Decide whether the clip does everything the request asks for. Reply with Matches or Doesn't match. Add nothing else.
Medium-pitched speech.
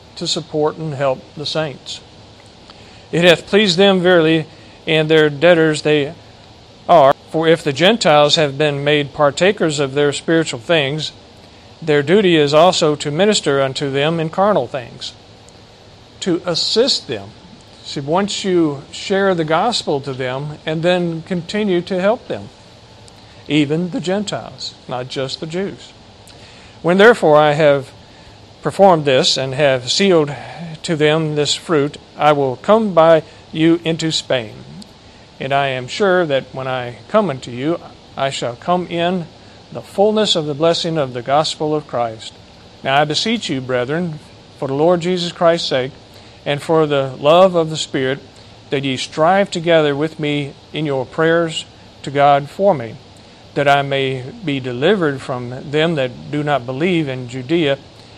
Matches